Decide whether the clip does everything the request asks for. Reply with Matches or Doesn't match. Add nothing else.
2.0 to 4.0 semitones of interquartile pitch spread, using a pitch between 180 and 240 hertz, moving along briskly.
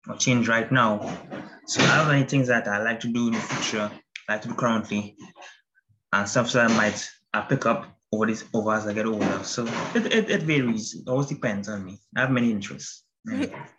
Doesn't match